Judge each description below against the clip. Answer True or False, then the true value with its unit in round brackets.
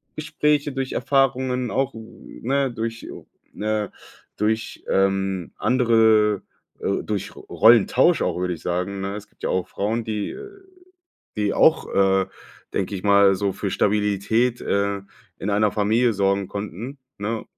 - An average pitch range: True (3.3 semitones)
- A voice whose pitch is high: False (105 Hz)